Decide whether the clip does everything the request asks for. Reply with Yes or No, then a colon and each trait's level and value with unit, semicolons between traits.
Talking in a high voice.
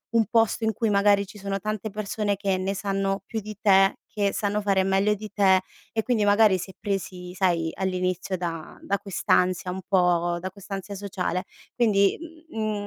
Yes: high, 195 Hz